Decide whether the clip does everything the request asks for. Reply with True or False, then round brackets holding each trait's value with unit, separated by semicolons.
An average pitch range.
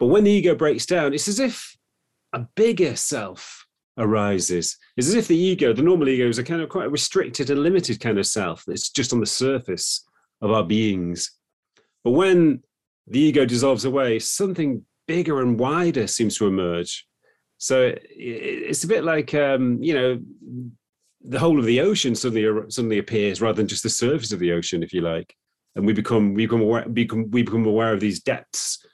False (5.8 semitones)